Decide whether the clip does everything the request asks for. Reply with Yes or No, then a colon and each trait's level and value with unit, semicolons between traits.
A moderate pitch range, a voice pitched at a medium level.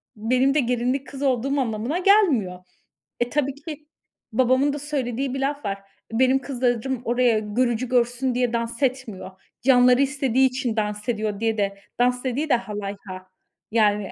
No: average, 3.2 semitones; very high, 250 Hz